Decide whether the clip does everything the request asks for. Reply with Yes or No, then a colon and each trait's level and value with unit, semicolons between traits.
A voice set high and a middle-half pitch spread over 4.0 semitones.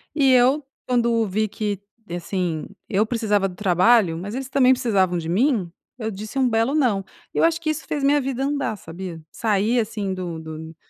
Yes: high, 215 Hz; wide, 5.5 semitones